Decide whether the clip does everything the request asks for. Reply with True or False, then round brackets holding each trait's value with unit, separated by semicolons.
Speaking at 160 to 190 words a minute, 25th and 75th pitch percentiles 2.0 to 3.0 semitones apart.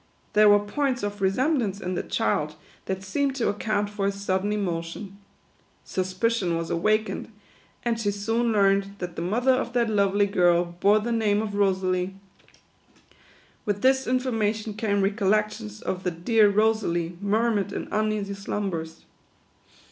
False (150 wpm; 2.5 semitones)